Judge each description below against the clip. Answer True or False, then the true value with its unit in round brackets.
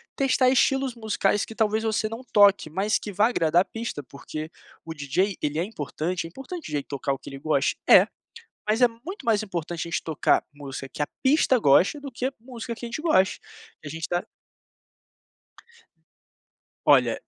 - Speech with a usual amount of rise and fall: False (7.0 semitones)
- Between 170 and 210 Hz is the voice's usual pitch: True (205 Hz)